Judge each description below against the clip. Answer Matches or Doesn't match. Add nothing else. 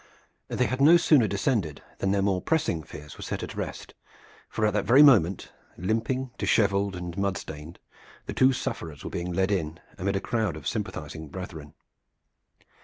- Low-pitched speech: Matches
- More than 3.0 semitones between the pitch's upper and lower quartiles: Matches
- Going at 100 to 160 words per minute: Doesn't match